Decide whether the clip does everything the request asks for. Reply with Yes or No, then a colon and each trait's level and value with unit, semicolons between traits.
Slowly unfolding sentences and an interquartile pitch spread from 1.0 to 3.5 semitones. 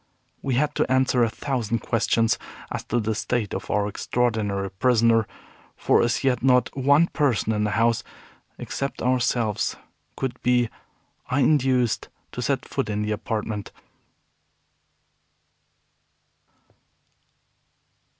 Yes: slow, 115 wpm; average, 3.0 semitones